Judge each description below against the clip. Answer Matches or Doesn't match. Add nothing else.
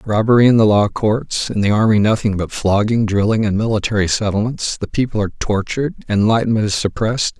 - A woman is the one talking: Doesn't match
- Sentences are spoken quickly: Doesn't match